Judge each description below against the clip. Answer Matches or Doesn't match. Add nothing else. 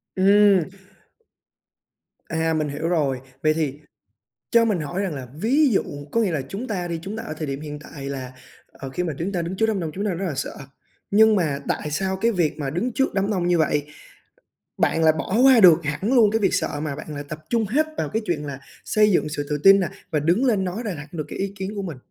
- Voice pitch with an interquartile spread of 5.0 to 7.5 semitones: Matches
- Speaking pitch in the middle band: Matches